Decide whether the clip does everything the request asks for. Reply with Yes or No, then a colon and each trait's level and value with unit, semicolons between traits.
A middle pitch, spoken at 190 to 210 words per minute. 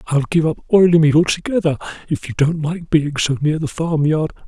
Yes: medium, 155 Hz; average, 200 wpm